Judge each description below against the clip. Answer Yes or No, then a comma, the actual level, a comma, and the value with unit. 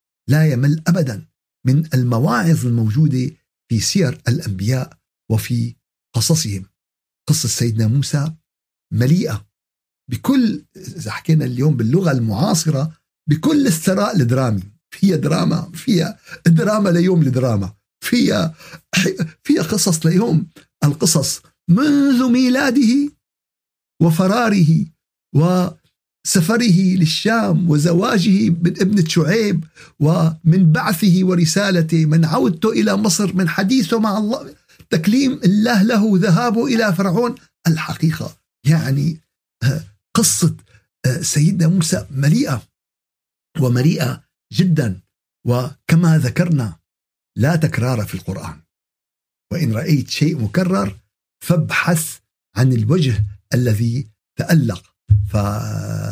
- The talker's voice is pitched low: No, medium, 160 Hz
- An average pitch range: No, wide, 7.3 semitones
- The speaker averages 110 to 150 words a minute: No, average, 95 wpm